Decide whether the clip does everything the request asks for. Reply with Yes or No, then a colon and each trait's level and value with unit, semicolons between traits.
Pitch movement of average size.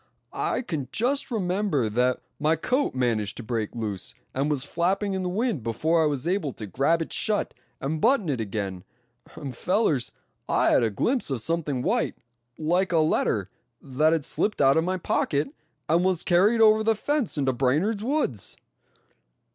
No: wide, 7.5 semitones